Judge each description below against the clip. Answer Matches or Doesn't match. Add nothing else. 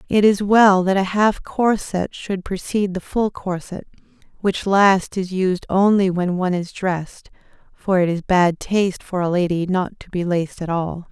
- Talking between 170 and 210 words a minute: Matches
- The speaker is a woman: Matches